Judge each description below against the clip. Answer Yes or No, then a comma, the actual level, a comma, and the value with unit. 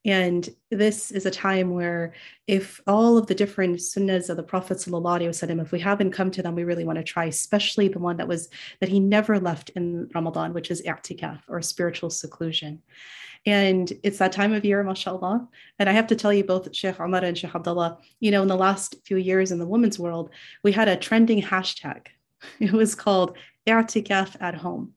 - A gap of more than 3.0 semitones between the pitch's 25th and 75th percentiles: No, average, 2.7 semitones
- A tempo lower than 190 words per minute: No, average, 200 wpm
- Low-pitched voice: No, medium, 185 Hz